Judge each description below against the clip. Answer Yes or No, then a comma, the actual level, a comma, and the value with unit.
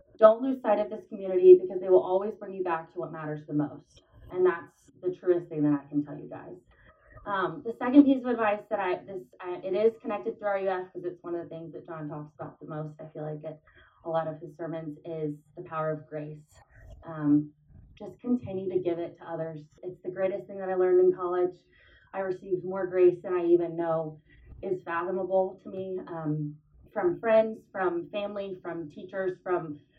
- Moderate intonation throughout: Yes, average, 3.3 semitones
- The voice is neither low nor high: Yes, medium, 180 Hz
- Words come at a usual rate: No, fast, 215 wpm